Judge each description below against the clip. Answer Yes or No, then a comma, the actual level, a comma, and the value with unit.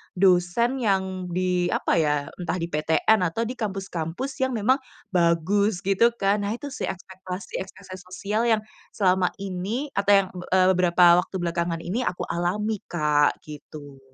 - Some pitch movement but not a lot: Yes, average, 3.1 semitones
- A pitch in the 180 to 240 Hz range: Yes, medium, 185 Hz